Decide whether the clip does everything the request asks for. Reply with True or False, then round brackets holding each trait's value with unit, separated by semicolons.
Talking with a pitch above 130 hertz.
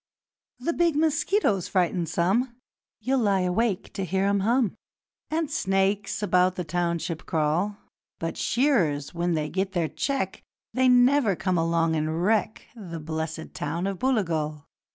True (190 Hz)